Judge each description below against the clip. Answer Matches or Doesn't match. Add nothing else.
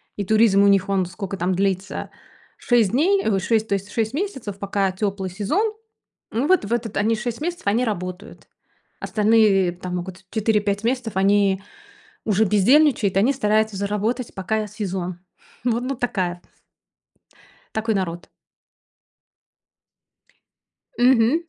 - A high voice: Matches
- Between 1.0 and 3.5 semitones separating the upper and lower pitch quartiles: Matches